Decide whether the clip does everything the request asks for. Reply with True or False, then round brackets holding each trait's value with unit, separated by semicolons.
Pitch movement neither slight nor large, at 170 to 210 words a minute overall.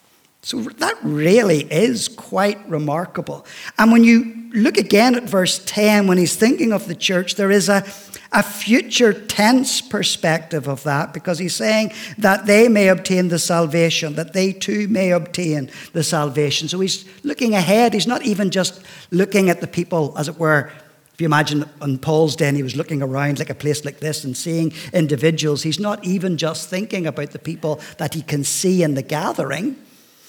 True (4.9 semitones; 185 wpm)